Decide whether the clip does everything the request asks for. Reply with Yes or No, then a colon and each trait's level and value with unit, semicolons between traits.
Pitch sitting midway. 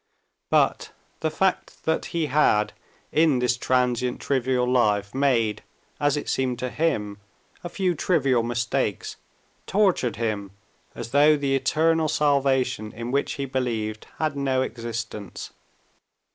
No: low, 130 Hz